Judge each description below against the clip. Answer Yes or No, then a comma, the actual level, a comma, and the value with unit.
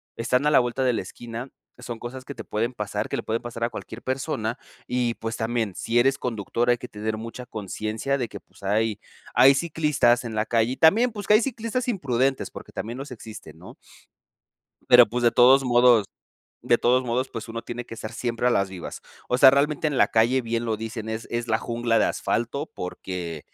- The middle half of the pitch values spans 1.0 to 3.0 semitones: Yes, narrow, 2.6 semitones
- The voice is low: Yes, low, 120 Hz